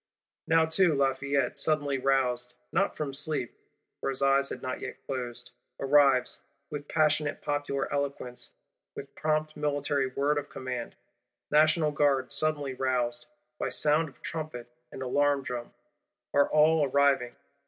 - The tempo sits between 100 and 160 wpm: Yes, slow, 135 wpm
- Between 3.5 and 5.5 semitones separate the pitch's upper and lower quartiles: No, narrow, 2.4 semitones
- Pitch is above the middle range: No, medium, 140 Hz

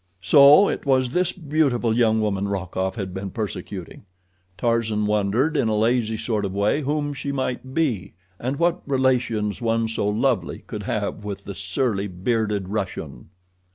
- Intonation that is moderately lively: Yes, average, 4.6 semitones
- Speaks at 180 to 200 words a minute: No, average, 155 wpm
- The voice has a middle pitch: No, low, 110 Hz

